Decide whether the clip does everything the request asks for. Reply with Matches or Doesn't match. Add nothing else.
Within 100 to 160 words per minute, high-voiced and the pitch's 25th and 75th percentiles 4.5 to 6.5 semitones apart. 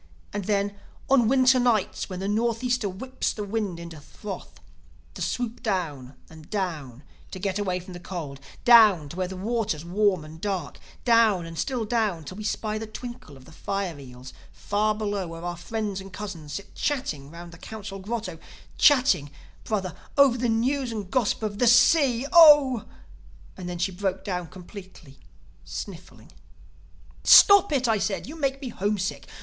Doesn't match